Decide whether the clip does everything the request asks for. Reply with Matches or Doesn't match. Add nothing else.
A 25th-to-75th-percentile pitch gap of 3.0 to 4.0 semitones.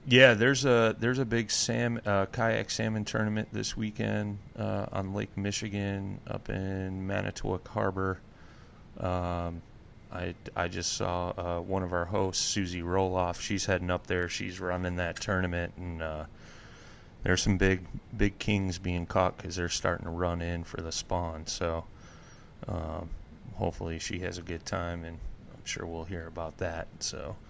Matches